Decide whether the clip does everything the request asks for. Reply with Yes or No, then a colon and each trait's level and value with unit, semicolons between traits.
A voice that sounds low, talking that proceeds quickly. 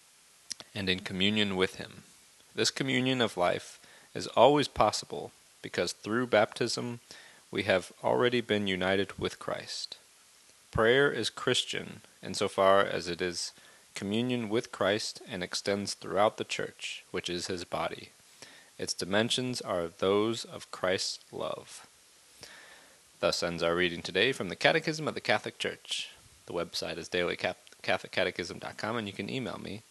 No: low, 100 Hz; average, 140 wpm